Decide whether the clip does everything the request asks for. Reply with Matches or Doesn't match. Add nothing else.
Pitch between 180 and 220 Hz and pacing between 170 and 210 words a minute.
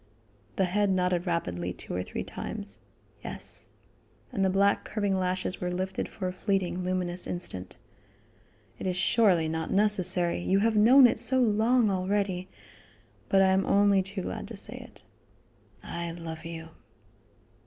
Doesn't match